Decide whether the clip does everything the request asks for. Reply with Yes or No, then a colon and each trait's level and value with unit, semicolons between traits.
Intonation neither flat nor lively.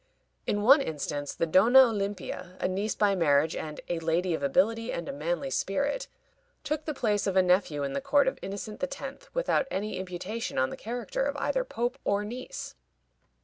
No: wide, 6.6 semitones